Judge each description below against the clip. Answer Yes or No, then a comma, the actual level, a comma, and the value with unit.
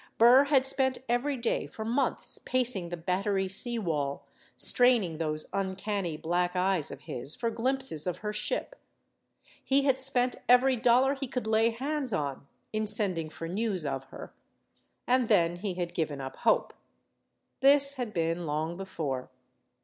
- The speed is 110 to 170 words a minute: Yes, average, 155 wpm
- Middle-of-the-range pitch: No, high, 210 Hz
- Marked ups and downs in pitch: Yes, wide, 6.8 semitones